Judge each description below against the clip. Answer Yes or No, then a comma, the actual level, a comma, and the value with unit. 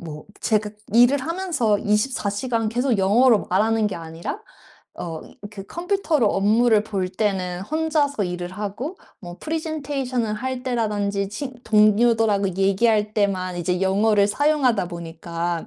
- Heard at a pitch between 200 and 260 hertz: Yes, high, 210 Hz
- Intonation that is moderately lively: Yes, average, 4.6 semitones